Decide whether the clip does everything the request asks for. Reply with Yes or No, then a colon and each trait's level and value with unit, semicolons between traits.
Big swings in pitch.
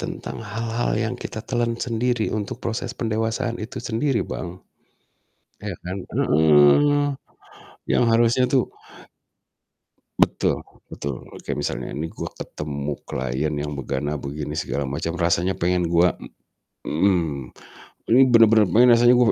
Yes: wide, 7.8 semitones